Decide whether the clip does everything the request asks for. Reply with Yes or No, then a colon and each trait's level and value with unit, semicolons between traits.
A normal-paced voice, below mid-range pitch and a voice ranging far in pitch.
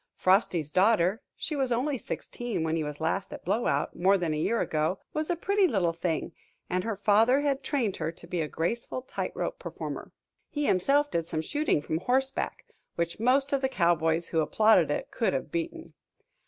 No: average, 195 wpm; high, 200 Hz; wide, 8.1 semitones